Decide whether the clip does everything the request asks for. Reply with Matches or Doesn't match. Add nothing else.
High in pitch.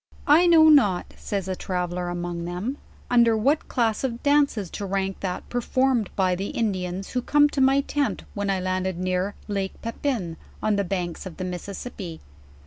Matches